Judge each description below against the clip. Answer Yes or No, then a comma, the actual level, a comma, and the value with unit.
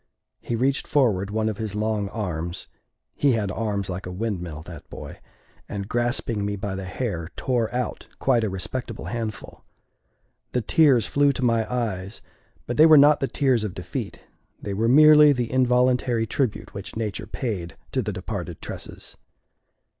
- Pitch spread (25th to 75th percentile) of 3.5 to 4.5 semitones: Yes, average, 4.2 semitones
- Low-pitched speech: Yes, low, 110 Hz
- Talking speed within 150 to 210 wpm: Yes, average, 165 wpm